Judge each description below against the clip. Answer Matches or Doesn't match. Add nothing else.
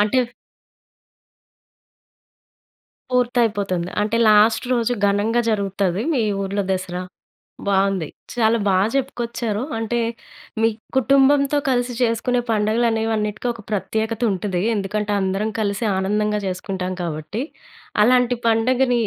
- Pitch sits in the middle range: Doesn't match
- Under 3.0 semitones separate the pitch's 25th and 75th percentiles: Doesn't match